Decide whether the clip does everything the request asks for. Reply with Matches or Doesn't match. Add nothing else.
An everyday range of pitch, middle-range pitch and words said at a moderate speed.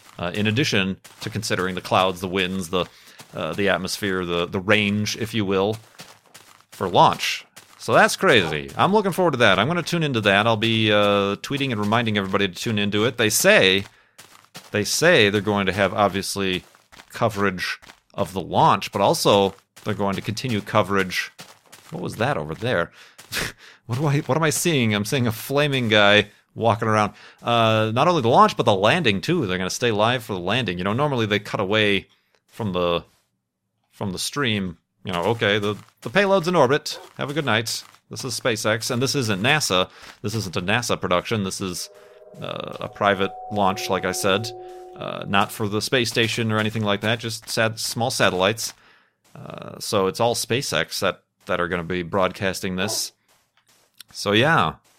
Doesn't match